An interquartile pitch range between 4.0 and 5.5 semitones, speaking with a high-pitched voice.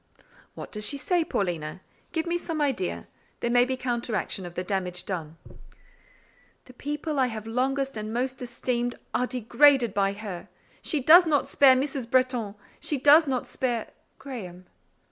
Yes: average, 5.0 semitones; very high, 250 Hz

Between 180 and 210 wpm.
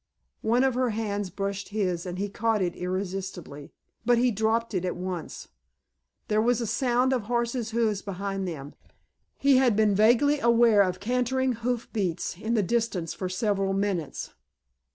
No: average, 165 wpm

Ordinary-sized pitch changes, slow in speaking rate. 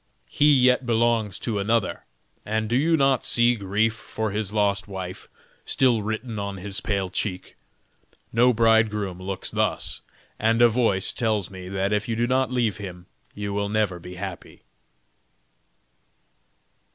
No: average, 3.0 semitones; average, 150 wpm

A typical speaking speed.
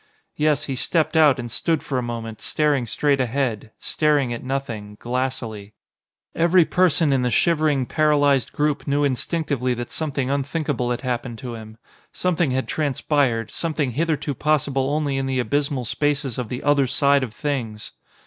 Yes: average, 160 wpm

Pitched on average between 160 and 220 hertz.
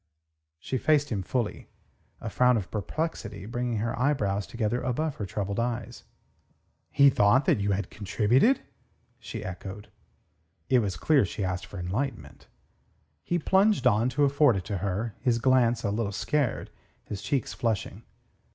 No: low, 115 Hz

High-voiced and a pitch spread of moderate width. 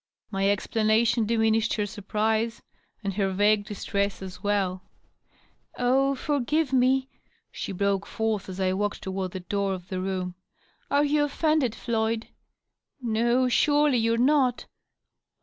Yes: high, 220 Hz; average, 4.1 semitones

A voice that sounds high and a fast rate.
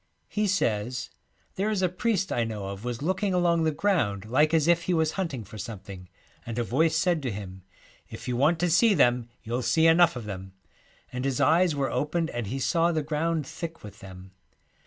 No: medium, 145 Hz; fast, 215 wpm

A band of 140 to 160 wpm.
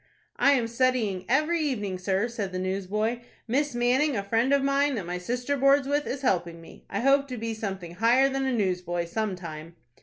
No: fast, 205 wpm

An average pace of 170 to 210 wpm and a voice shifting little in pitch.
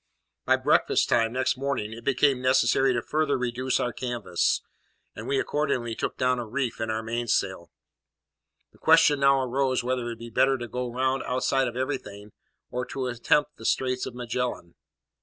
Yes: average, 175 wpm; narrow, 2.1 semitones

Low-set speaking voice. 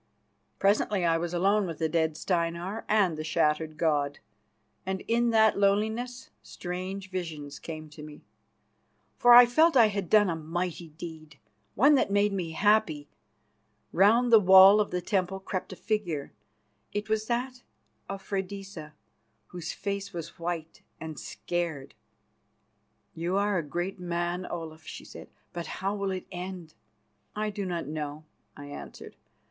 No: medium, 180 Hz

